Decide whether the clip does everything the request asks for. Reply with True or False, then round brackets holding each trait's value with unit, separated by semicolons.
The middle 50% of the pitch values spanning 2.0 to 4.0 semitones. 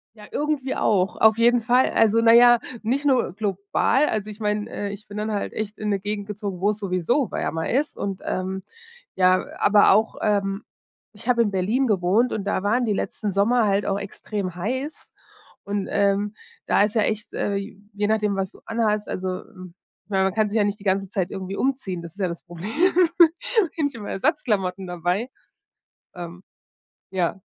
True (2.9 semitones)